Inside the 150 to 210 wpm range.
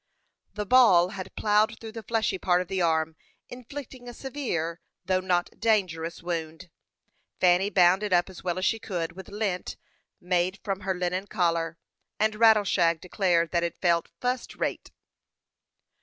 Yes: average, 155 wpm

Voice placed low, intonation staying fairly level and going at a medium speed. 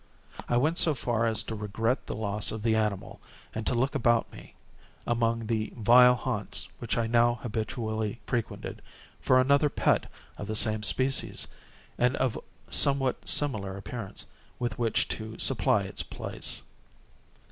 Yes: low, 115 Hz; narrow, 2.3 semitones; average, 150 wpm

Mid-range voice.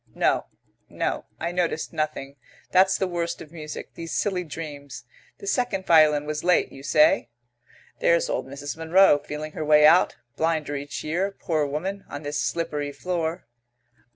Yes: medium, 155 Hz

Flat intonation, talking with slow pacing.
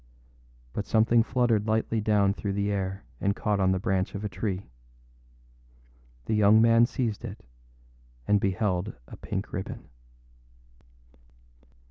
Yes: narrow, 2.3 semitones; slow, 130 wpm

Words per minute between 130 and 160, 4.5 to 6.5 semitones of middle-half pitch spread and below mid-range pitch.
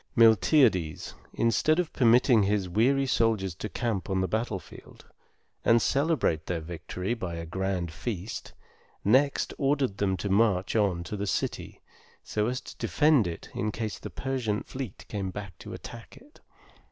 Yes: average, 155 wpm; average, 4.8 semitones; low, 105 Hz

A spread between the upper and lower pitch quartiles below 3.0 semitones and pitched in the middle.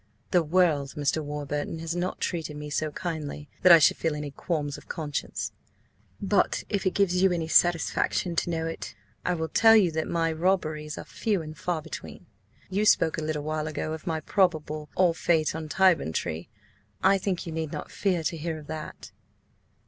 Yes: narrow, 2.6 semitones; medium, 160 Hz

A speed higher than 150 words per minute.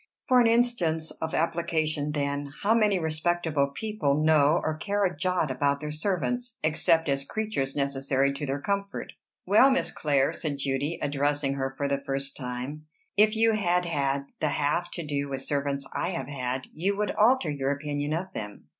Yes: average, 180 wpm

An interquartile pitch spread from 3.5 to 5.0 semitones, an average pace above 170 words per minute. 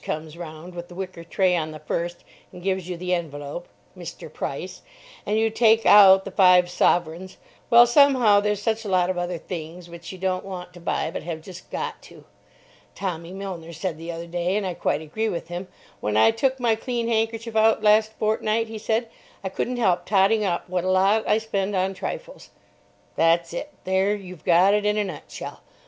Yes: average, 3.8 semitones; average, 200 wpm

